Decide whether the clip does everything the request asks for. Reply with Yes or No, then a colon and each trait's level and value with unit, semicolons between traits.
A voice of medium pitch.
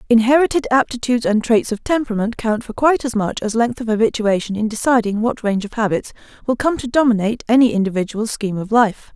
No: high, 230 Hz